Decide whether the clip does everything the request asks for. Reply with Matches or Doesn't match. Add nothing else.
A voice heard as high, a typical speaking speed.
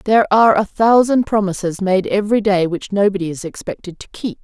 Matches